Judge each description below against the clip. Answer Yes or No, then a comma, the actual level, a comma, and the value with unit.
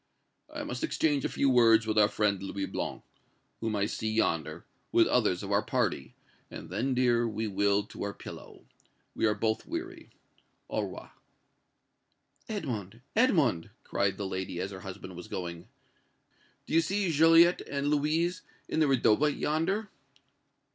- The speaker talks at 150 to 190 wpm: Yes, average, 155 wpm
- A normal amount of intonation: No, wide, 7.6 semitones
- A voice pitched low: Yes, low, 115 Hz